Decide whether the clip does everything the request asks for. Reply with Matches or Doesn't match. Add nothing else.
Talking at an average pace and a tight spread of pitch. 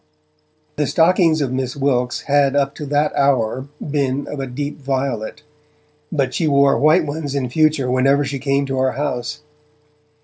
Matches